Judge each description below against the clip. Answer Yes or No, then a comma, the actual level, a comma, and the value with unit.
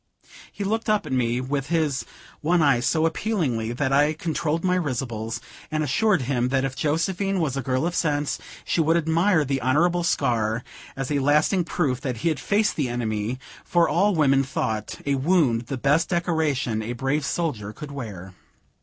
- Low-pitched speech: No, medium, 145 Hz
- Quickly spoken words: No, average, 180 wpm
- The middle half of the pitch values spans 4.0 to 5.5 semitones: Yes, average, 4.8 semitones